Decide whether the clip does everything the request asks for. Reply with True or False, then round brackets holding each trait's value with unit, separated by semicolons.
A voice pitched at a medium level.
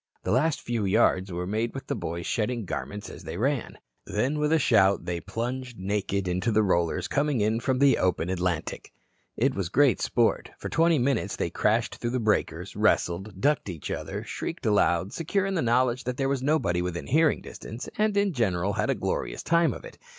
False (115 Hz)